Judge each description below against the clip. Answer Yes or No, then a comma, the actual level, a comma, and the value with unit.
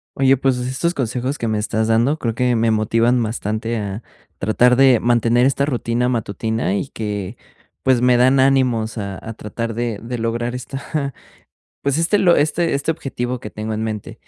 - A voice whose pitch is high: No, low, 120 Hz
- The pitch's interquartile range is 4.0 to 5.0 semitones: No, average, 2.9 semitones